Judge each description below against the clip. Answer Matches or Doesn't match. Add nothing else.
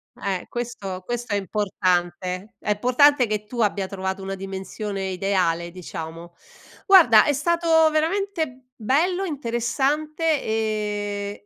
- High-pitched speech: Matches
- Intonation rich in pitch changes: Matches